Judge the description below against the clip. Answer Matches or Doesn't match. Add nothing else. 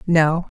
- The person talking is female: Matches